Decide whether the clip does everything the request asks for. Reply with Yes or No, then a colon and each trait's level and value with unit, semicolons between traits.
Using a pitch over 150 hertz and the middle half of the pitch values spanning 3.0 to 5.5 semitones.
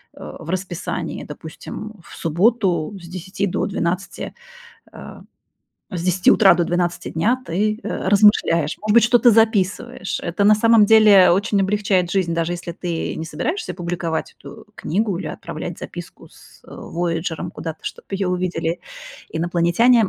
Yes: medium, 185 Hz; average, 3.6 semitones